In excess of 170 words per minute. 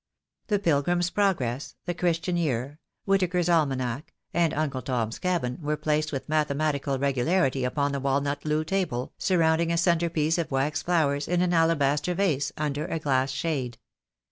No: average, 150 wpm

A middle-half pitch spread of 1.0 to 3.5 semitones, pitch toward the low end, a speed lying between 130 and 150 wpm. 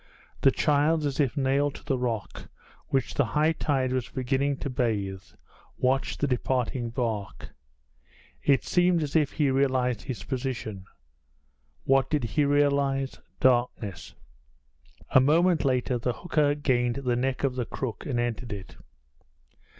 Yes: average, 2.8 semitones; low, 130 Hz; average, 140 wpm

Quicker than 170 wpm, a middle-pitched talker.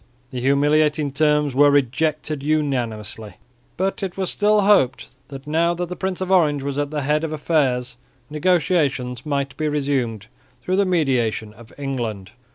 No: average, 160 wpm; medium, 145 Hz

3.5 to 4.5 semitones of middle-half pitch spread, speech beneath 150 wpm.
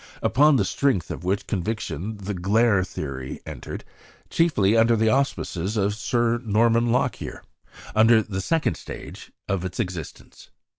Yes: average, 3.8 semitones; average, 140 wpm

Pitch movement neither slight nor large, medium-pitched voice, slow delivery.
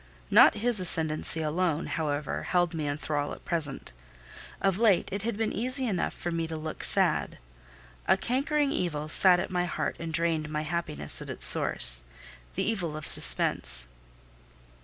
No: average, 3.9 semitones; medium, 165 Hz; average, 160 wpm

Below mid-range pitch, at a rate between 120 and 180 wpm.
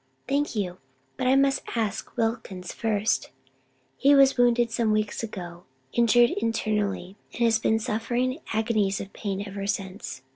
No: high, 220 Hz; average, 145 wpm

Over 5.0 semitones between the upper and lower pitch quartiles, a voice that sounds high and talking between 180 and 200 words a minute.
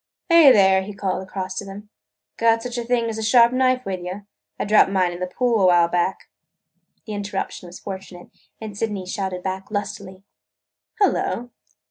No: average, 3.4 semitones; high, 200 Hz; average, 185 wpm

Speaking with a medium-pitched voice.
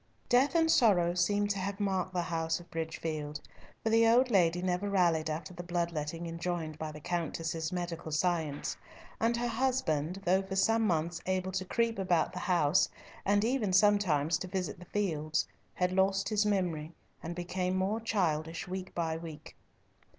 Yes: medium, 180 Hz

